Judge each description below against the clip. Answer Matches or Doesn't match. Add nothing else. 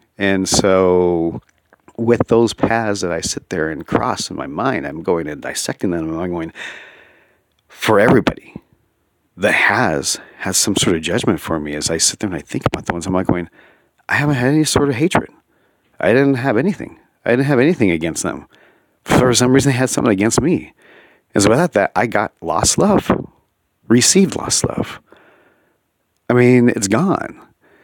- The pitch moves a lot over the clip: Matches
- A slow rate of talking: Doesn't match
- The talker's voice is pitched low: Matches